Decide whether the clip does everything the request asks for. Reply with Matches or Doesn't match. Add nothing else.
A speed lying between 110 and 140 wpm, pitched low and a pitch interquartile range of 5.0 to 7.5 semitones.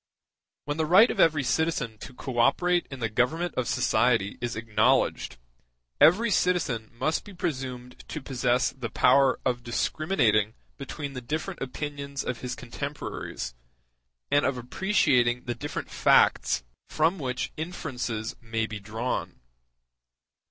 Doesn't match